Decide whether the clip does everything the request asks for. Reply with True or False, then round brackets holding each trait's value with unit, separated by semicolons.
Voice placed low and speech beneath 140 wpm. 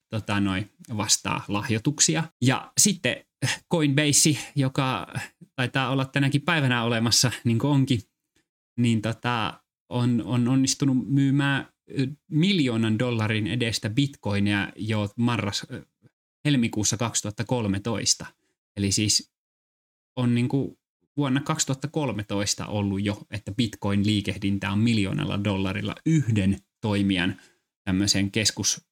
True (115 Hz; 100 wpm)